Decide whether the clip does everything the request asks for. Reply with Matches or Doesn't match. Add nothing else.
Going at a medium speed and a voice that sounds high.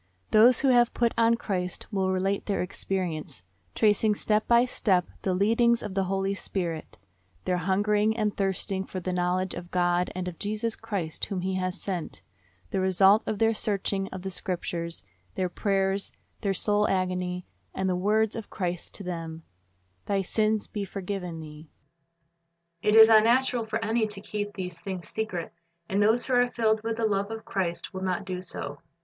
Matches